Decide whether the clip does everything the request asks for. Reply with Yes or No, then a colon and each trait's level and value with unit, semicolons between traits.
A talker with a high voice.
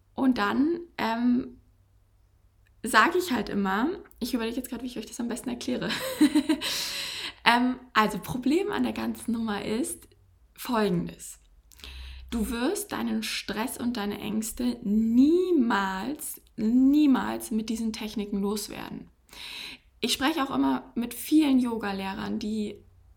Yes: high, 225 Hz